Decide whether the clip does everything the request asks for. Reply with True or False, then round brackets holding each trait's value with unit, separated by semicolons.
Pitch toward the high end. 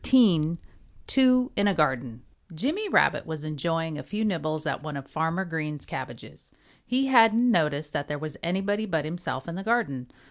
False (165 Hz)